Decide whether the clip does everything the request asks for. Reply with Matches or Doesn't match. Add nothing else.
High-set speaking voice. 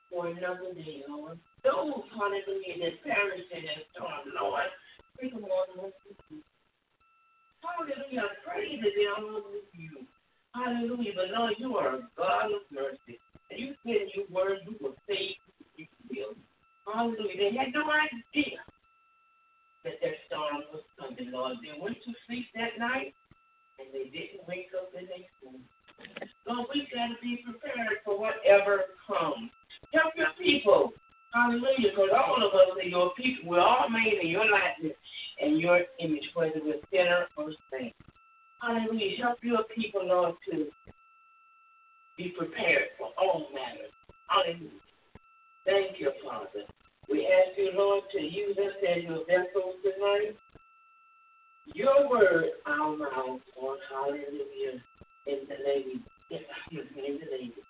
Matches